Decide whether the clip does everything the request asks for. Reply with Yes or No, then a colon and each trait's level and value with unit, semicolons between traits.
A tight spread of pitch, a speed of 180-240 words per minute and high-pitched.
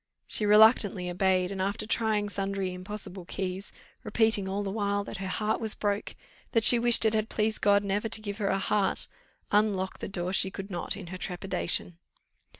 Yes: narrow, 2.0 semitones; average, 190 wpm; high, 200 Hz